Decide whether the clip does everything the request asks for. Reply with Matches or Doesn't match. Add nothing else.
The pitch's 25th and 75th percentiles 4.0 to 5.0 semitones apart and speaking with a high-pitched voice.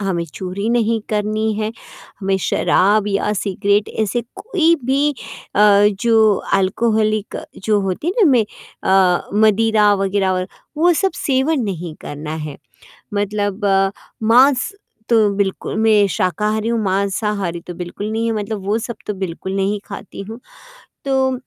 Doesn't match